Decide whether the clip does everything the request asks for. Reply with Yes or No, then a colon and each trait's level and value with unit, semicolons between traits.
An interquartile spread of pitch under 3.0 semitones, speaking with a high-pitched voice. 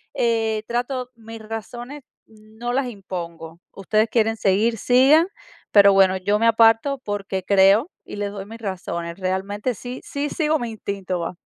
No: average, 3.6 semitones; high, 215 Hz